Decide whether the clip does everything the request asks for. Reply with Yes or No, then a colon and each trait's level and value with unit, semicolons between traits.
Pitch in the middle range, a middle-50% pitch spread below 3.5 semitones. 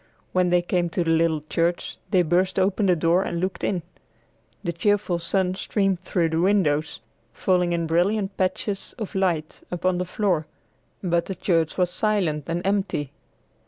Yes: medium, 180 Hz; narrow, 2.4 semitones